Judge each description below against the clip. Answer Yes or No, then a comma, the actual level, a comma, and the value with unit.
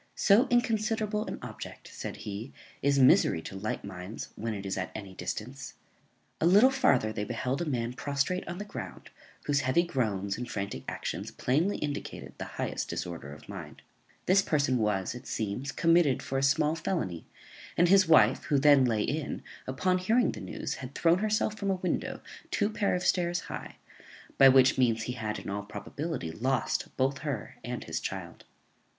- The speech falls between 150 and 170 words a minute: No, average, 180 wpm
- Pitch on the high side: No, low, 135 Hz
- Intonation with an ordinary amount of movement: No, wide, 8.3 semitones